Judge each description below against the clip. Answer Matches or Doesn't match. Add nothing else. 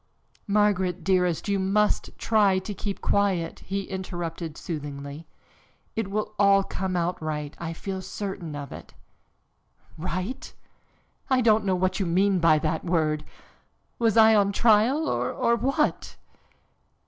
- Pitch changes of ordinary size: Matches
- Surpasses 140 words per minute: Doesn't match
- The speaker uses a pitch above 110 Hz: Matches